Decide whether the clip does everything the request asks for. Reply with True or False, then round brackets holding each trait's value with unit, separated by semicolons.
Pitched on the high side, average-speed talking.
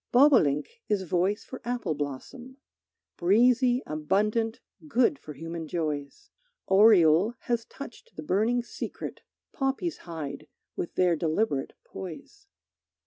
False (200 Hz; 110 wpm)